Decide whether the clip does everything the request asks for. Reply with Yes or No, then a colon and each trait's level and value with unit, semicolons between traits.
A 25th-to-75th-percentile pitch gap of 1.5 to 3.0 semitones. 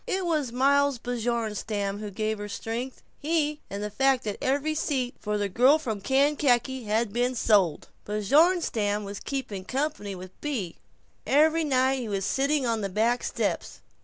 No: average, 5.2 semitones